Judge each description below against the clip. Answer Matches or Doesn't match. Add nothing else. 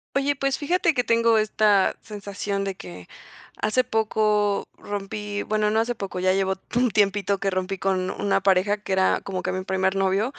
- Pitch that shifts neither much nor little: Doesn't match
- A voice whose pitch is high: Matches